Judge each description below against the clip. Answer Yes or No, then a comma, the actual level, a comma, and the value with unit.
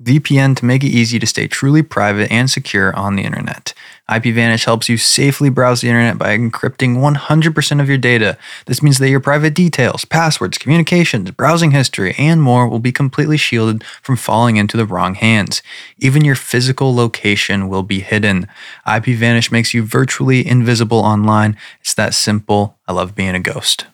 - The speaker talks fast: No, average, 175 wpm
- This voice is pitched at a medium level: No, low, 120 Hz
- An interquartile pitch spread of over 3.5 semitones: Yes, average, 4.2 semitones